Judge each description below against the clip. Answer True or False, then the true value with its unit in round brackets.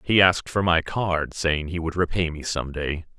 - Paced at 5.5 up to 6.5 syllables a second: False (4.7 syllables/s)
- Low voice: True (85 Hz)